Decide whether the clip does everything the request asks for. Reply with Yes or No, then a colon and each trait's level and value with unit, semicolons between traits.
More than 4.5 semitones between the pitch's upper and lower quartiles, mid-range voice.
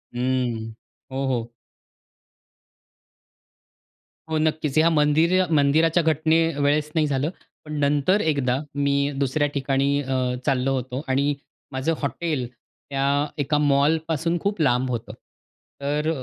No: average, 2.9 semitones; medium, 145 Hz